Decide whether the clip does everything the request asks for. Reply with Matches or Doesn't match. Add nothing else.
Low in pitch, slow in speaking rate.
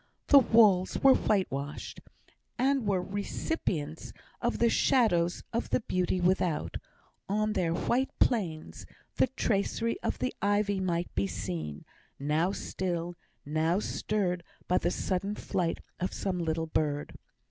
Doesn't match